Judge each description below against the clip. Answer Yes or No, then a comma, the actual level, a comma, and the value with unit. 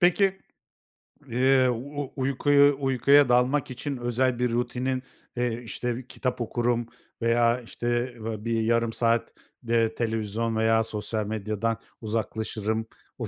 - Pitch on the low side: Yes, low, 120 Hz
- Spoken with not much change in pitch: Yes, narrow, 2.3 semitones